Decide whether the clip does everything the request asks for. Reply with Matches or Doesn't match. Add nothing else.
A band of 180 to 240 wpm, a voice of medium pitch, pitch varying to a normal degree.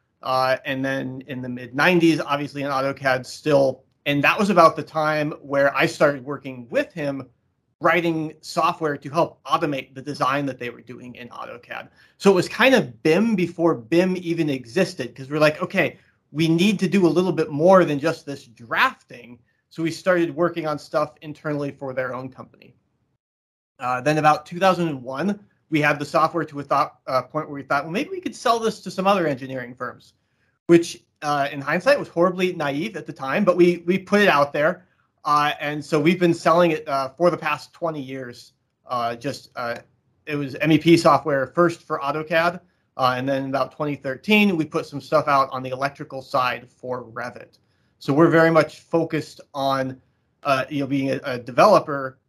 Matches